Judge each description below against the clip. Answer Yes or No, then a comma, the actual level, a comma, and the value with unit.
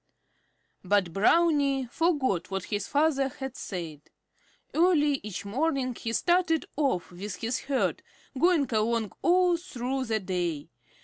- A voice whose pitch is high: Yes, very high, 260 Hz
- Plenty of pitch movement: Yes, wide, 7.3 semitones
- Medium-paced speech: No, slow, 125 wpm